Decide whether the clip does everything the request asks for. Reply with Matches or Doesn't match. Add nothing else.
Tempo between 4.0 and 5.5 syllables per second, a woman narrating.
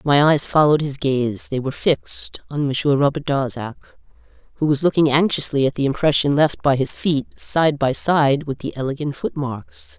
Matches